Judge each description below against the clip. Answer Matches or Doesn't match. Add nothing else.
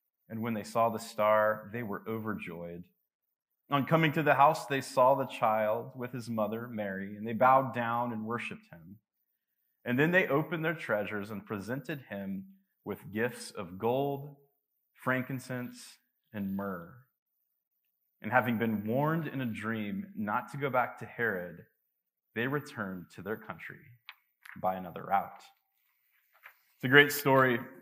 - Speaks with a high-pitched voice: Doesn't match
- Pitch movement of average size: Matches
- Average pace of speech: Matches